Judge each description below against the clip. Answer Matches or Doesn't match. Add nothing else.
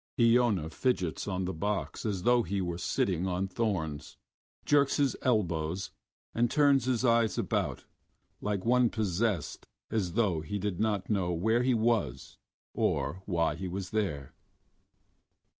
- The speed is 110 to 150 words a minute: Matches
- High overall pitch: Doesn't match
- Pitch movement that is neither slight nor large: Matches